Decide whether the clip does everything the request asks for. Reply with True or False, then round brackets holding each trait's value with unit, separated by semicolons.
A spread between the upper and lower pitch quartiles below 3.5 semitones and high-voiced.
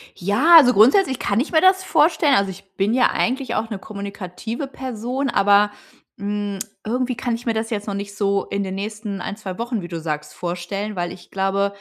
False (3.8 semitones; 210 Hz)